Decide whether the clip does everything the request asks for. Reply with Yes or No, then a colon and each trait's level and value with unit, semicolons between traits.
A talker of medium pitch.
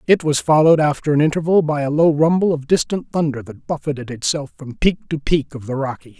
Yes: medium, 145 Hz